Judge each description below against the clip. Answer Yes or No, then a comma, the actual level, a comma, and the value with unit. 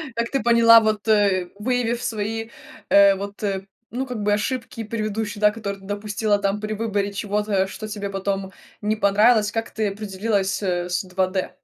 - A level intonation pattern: Yes, narrow, 2.0 semitones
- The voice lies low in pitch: No, high, 210 Hz